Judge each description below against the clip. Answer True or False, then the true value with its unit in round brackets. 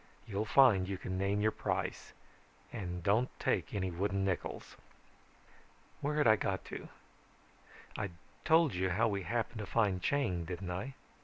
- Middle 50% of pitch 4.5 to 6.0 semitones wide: False (3.5 semitones)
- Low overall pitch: True (100 Hz)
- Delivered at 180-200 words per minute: False (155 wpm)